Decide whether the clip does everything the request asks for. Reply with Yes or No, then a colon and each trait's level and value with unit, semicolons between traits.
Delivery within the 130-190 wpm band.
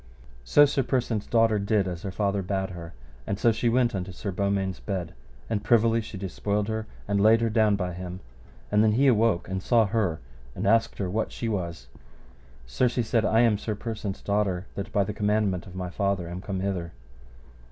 No: fast, 205 wpm